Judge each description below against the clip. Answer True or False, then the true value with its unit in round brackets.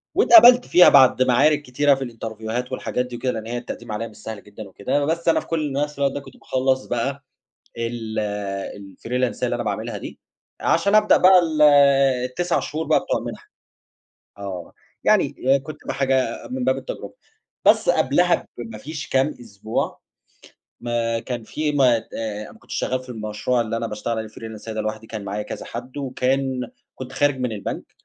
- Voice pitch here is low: True (125 Hz)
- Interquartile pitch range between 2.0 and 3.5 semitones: False (4.2 semitones)